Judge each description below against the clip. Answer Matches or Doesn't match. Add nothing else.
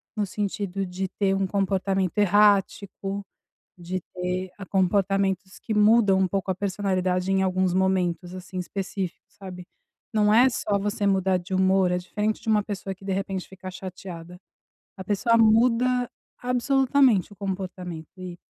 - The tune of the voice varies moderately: Doesn't match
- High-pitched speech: Matches